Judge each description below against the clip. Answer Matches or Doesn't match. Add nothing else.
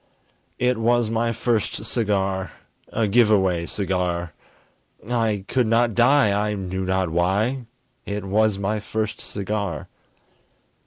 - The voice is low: Matches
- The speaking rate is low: Matches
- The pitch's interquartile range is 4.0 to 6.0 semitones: Doesn't match